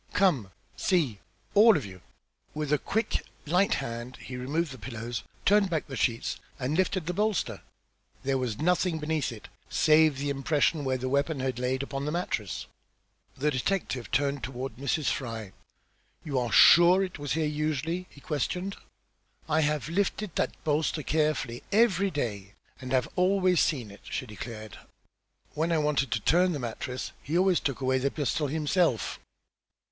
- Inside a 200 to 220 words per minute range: No, average, 165 wpm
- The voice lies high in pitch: No, medium, 145 Hz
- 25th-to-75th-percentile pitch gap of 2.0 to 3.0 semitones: No, average, 4.8 semitones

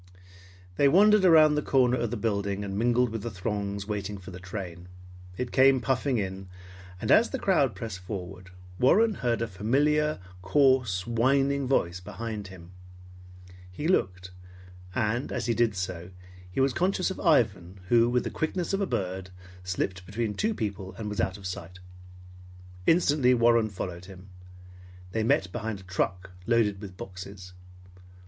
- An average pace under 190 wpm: Yes, average, 160 wpm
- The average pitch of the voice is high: No, low, 110 Hz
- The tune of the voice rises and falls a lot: Yes, wide, 5.8 semitones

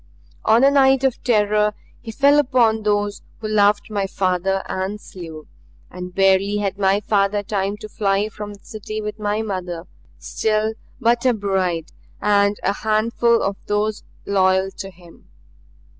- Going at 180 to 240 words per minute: No, average, 155 wpm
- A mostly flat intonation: Yes, narrow, 2.0 semitones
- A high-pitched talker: Yes, high, 205 Hz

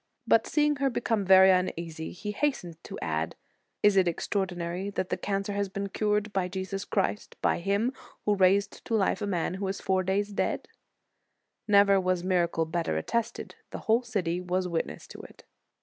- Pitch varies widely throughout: No, narrow, 2.5 semitones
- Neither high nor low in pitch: No, high, 195 Hz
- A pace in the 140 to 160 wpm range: No, average, 185 wpm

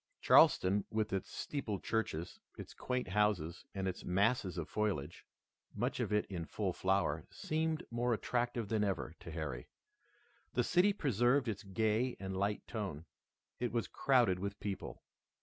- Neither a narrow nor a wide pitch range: Yes, average, 4.3 semitones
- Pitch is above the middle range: No, low, 105 Hz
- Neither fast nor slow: Yes, average, 150 wpm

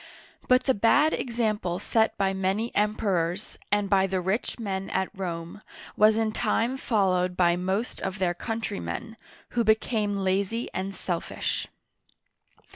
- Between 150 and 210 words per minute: No, slow, 135 wpm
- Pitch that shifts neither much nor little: Yes, average, 3.0 semitones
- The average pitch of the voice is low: No, high, 200 Hz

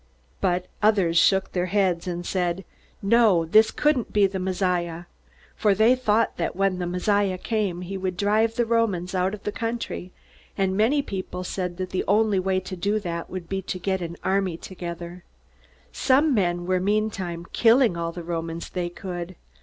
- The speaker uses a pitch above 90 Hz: Yes, high, 190 Hz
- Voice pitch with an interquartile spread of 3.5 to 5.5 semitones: No, average, 3.0 semitones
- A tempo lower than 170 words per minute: No, average, 175 wpm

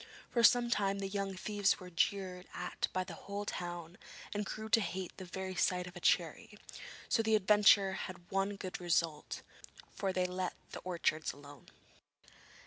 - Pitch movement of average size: No, narrow, 2.1 semitones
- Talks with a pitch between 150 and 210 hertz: Yes, high, 190 Hz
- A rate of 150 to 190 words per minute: Yes, average, 170 wpm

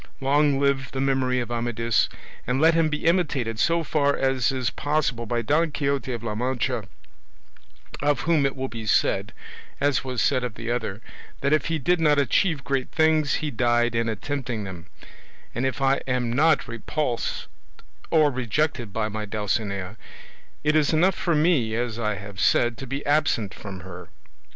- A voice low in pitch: Yes, low, 130 Hz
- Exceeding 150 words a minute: Yes, average, 175 wpm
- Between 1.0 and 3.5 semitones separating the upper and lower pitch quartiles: No, average, 4.1 semitones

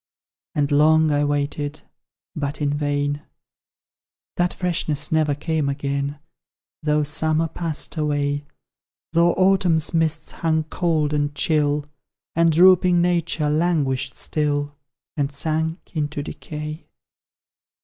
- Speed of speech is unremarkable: No, slow, 110 wpm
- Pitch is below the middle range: No, medium, 150 Hz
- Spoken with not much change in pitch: Yes, narrow, 1.9 semitones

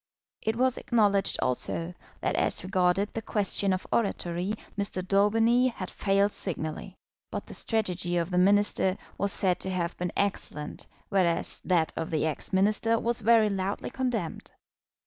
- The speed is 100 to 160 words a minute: Yes, average, 150 wpm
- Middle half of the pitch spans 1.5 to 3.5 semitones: Yes, average, 3.1 semitones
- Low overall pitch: No, high, 195 Hz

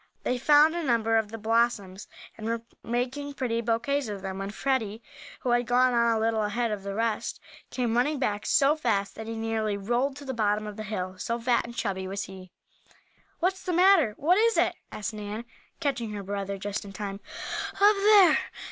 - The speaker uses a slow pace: No, average, 200 wpm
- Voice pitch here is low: No, high, 230 Hz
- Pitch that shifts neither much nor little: Yes, average, 4.2 semitones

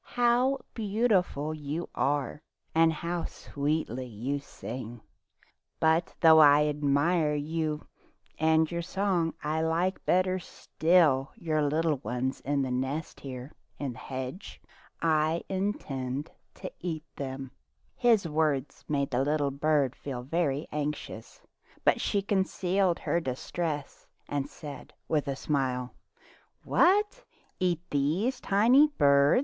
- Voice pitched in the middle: Yes, medium, 155 Hz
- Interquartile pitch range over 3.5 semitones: Yes, average, 3.9 semitones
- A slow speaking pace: Yes, slow, 125 wpm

